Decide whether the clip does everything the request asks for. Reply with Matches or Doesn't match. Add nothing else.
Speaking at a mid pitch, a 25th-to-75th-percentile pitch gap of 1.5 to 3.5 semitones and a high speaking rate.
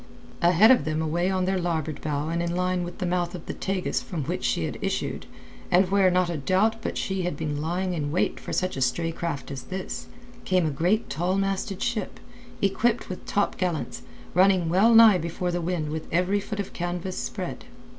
Doesn't match